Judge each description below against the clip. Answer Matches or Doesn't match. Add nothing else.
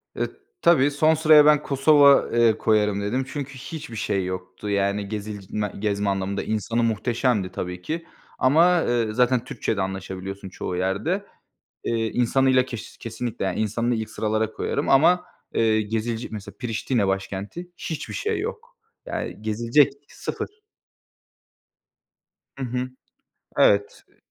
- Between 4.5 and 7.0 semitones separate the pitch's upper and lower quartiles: Matches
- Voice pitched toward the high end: Doesn't match